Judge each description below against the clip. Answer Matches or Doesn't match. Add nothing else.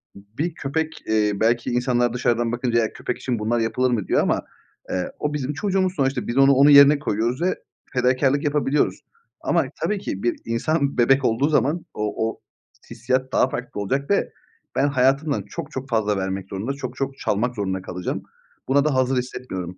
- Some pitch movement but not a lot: Matches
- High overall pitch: Doesn't match